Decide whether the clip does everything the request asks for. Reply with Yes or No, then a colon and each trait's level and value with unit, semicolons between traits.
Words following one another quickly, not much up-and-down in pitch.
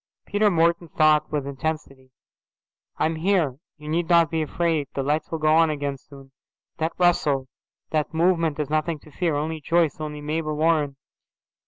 No: average, 165 wpm; narrow, 2.1 semitones